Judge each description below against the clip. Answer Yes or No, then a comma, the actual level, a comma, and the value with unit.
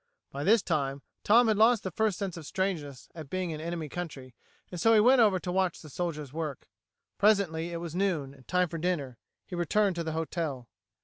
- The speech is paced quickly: Yes, fast, 215 wpm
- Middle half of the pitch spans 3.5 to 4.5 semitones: Yes, average, 4.1 semitones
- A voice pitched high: No, medium, 170 Hz